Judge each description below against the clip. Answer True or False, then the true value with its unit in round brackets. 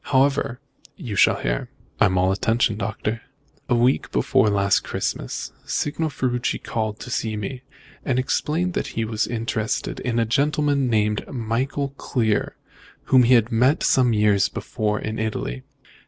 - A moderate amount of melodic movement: True (3.4 semitones)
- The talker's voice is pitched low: True (115 Hz)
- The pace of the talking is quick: False (150 wpm)